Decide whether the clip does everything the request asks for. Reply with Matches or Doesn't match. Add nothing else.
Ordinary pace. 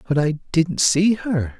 Matches